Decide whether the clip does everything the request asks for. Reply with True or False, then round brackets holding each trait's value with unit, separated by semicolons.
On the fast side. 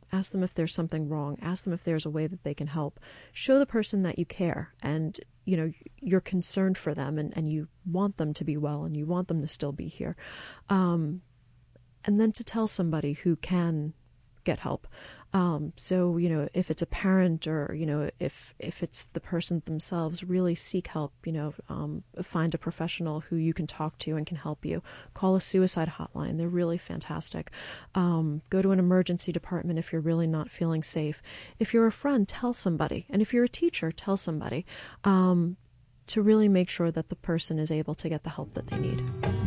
True (210 wpm)